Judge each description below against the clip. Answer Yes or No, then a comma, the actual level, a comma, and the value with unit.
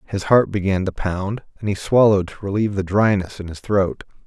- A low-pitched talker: Yes, low, 100 Hz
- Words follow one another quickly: Yes, fast, 210 wpm